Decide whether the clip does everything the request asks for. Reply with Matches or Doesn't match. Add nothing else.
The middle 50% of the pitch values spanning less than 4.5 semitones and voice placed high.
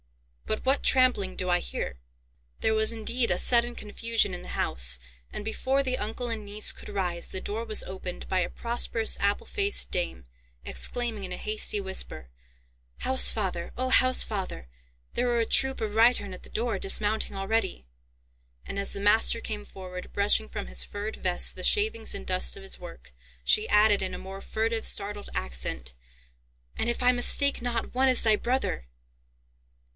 Matches